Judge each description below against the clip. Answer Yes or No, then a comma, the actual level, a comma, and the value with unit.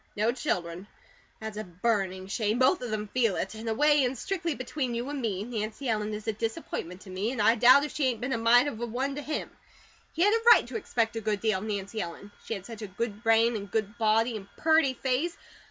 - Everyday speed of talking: No, fast, 250 wpm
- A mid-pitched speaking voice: No, high, 225 Hz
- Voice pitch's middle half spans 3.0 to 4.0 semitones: Yes, average, 3.5 semitones